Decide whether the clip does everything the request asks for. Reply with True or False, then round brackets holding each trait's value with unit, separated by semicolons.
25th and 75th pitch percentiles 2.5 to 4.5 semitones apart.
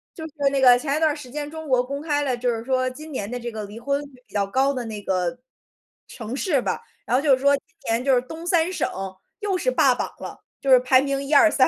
True (3.1 semitones)